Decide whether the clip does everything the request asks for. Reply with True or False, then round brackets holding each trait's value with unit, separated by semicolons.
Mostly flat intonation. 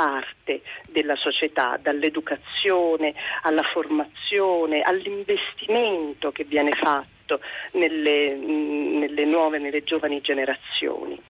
True (2.0 semitones)